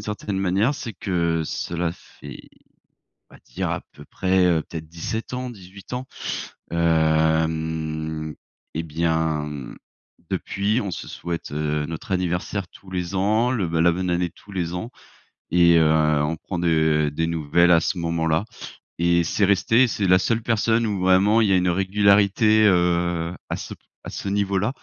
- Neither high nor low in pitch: No, very low, 90 Hz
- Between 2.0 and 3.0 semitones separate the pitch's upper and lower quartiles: No, average, 3.5 semitones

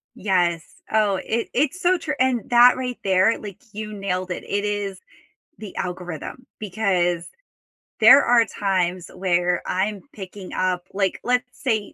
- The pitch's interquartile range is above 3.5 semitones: Yes, average, 4.0 semitones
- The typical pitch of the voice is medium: No, high, 200 Hz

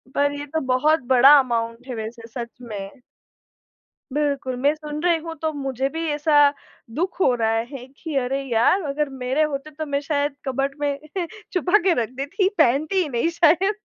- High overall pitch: Yes, very high, 280 Hz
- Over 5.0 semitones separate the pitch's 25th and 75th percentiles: No, average, 3.4 semitones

